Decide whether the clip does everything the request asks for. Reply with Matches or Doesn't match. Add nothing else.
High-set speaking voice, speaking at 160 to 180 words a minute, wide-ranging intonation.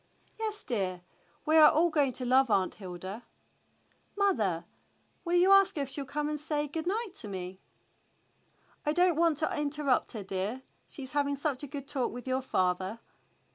Matches